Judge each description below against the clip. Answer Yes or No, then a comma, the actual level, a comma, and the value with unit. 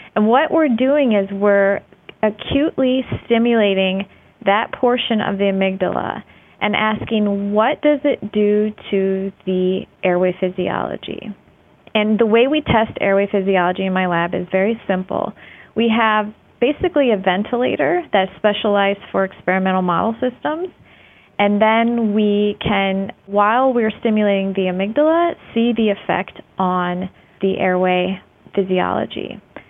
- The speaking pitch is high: Yes, high, 205 Hz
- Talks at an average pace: No, slow, 125 wpm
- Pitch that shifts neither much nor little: Yes, average, 3.2 semitones